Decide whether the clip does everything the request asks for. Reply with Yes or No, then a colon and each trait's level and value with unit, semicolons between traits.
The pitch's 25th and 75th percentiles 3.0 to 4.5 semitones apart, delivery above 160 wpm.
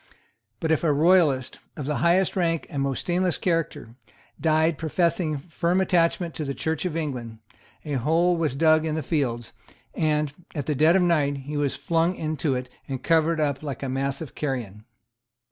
Yes: average, 3.3 semitones; average, 180 wpm